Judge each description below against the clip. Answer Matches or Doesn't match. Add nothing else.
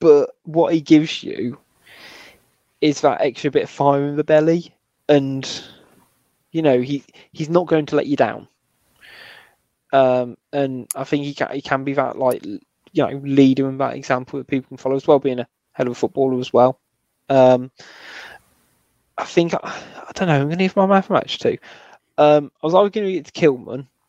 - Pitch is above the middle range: Doesn't match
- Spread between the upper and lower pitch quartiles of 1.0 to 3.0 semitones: Matches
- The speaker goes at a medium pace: Matches